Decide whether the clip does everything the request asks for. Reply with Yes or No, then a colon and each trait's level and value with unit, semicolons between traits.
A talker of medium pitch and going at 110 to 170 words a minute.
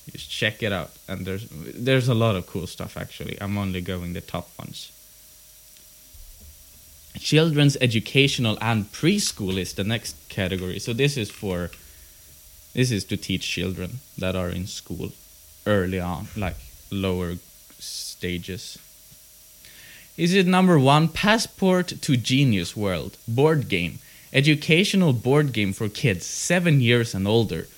No: low, 100 Hz; average, 140 wpm